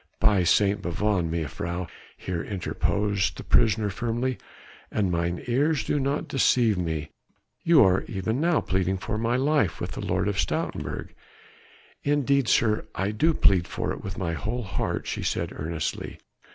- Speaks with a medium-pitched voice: No, low, 105 Hz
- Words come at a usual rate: Yes, average, 155 wpm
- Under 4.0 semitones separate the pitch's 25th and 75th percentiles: No, wide, 5.4 semitones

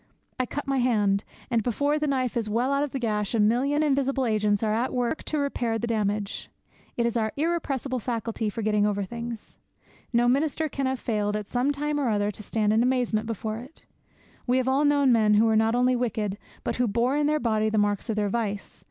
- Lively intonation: No, average, 3.7 semitones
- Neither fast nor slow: No, fast, 225 wpm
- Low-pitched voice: No, high, 235 Hz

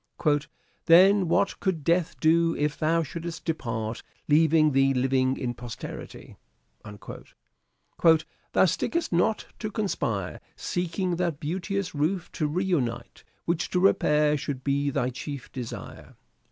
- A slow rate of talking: Yes, slow, 130 wpm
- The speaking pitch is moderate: Yes, medium, 160 Hz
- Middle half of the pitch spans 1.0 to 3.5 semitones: No, average, 4.2 semitones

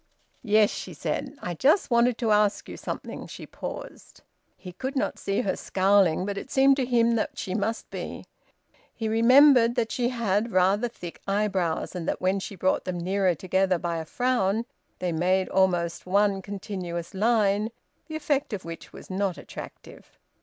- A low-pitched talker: No, high, 200 Hz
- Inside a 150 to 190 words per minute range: Yes, average, 175 wpm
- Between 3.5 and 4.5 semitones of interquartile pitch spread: Yes, average, 4.0 semitones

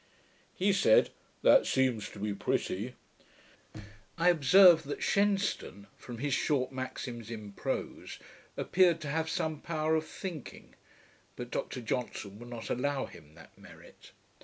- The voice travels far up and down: Yes, wide, 5.9 semitones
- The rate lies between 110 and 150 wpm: Yes, average, 140 wpm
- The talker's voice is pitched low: Yes, low, 130 Hz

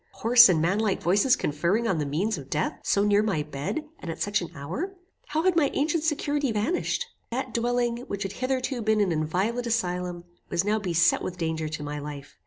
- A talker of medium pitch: No, high, 205 Hz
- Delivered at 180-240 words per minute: Yes, average, 200 wpm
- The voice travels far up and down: Yes, wide, 6.7 semitones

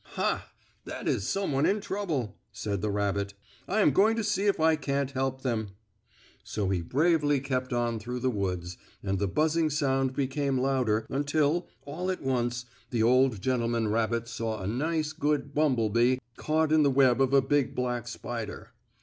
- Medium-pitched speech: No, low, 130 Hz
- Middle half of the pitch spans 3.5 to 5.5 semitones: Yes, average, 4.5 semitones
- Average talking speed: Yes, average, 175 wpm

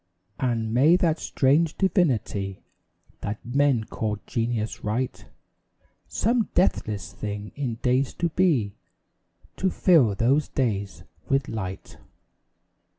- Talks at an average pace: No, slow, 105 wpm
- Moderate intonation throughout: No, wide, 6.0 semitones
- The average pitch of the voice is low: Yes, low, 125 Hz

